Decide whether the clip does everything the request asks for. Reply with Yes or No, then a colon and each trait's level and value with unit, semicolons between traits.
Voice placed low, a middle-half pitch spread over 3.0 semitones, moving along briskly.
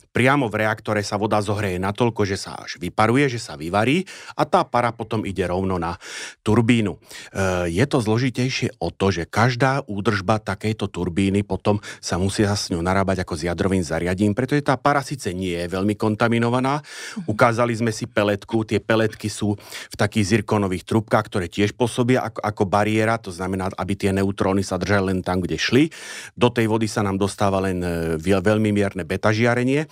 Yes: low, 105 Hz; average, 3.5 semitones; fast, 180 wpm